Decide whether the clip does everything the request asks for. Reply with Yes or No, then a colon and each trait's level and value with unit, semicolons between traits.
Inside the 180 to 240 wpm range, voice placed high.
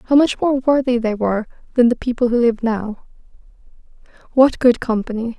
No: average, 155 wpm; high, 240 Hz